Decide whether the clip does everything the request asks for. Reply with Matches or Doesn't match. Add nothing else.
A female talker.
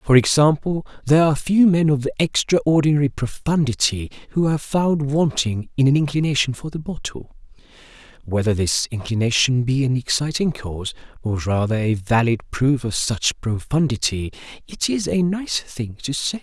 Doesn't match